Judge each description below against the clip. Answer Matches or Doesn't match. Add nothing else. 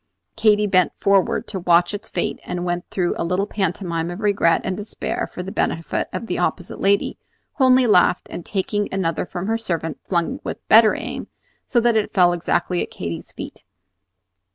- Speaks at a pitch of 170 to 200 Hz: Matches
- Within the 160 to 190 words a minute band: Matches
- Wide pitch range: Doesn't match